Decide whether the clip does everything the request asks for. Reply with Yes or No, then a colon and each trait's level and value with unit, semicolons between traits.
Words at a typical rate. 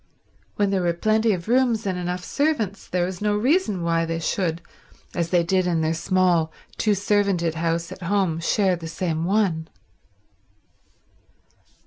Yes: average, 155 wpm